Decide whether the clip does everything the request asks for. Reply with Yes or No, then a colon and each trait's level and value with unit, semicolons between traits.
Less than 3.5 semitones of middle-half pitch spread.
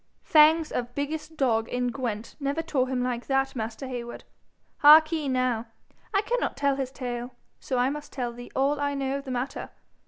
Yes: average, 2.8 semitones